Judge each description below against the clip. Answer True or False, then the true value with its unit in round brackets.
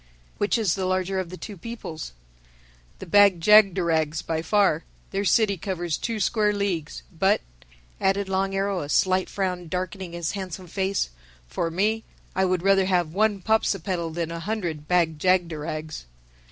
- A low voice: False (185 Hz)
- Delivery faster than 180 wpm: False (155 wpm)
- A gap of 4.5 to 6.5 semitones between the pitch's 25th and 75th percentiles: False (3.0 semitones)